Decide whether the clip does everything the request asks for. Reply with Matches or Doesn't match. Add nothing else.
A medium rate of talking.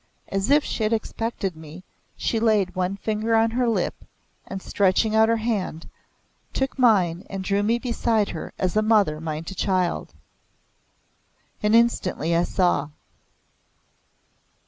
Matches